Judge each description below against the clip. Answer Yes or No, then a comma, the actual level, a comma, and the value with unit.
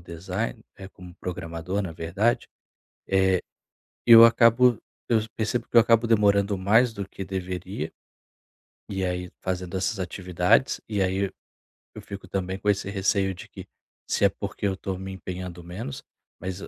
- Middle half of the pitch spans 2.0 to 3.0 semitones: Yes, narrow, 2.4 semitones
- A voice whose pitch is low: Yes, very low, 95 Hz